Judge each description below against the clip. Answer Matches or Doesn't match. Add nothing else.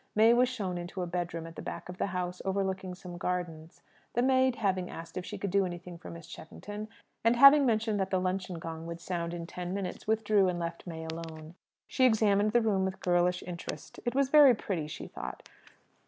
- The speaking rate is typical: Doesn't match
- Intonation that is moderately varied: Matches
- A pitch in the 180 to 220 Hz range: Matches